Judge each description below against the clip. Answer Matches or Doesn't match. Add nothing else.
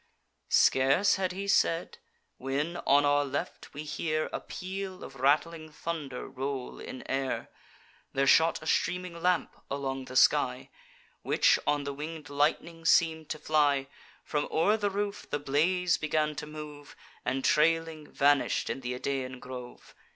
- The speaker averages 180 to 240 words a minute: Doesn't match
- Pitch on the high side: Doesn't match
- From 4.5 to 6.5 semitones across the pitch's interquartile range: Doesn't match